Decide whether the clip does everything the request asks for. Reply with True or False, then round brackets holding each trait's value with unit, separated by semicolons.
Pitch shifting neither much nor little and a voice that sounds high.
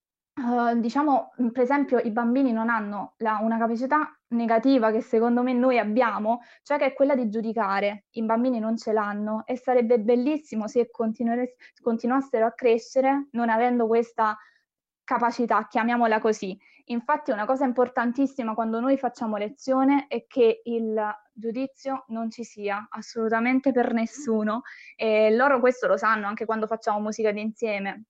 False (2.3 semitones; 235 Hz)